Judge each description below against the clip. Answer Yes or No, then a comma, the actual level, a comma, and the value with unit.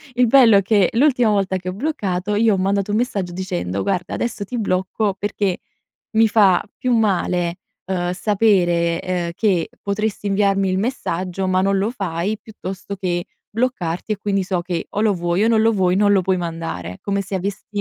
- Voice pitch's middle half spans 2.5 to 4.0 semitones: Yes, average, 2.8 semitones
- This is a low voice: No, high, 195 Hz